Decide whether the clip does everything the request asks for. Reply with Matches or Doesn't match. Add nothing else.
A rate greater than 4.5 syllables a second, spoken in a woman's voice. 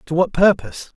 Doesn't match